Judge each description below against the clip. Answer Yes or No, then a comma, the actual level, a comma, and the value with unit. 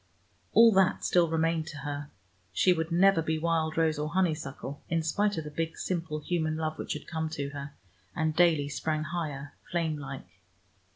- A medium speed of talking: Yes, average, 180 wpm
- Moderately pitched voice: Yes, medium, 160 Hz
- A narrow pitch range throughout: Yes, narrow, 1.9 semitones